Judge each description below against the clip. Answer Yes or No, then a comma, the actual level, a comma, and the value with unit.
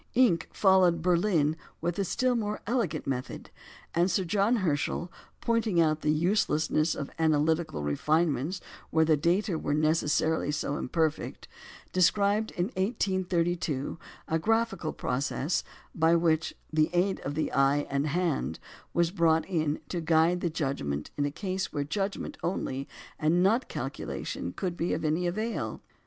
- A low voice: No, medium, 165 Hz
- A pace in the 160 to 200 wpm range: No, average, 145 wpm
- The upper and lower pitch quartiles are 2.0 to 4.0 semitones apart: Yes, average, 3.6 semitones